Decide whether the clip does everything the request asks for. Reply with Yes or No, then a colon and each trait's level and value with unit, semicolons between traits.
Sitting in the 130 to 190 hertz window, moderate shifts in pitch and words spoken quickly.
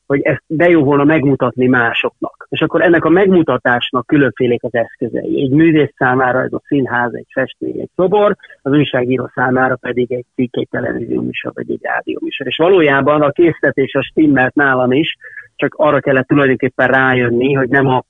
Yes: low, 135 Hz; average, 3.8 semitones; fast, 180 wpm